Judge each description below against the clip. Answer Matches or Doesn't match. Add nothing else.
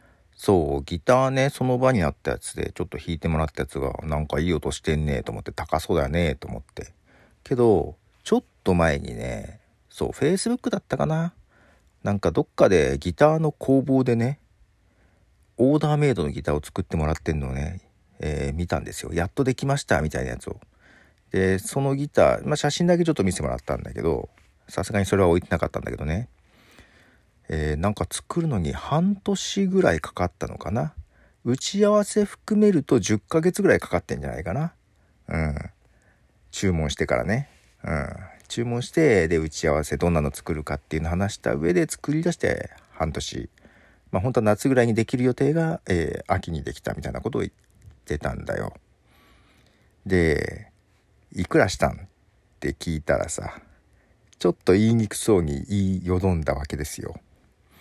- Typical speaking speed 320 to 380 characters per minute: Matches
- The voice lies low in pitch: Matches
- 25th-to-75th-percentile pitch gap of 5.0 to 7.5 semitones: Doesn't match